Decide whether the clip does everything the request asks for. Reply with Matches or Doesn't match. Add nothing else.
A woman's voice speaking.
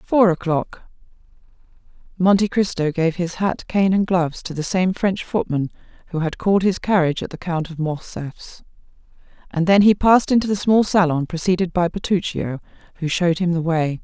Matches